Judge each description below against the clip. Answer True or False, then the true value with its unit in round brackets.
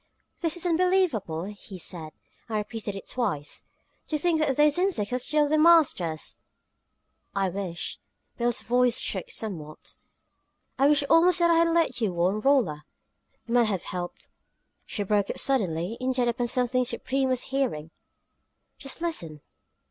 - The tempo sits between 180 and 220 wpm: False (155 wpm)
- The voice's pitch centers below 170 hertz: False (240 Hz)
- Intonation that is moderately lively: False (7.5 semitones)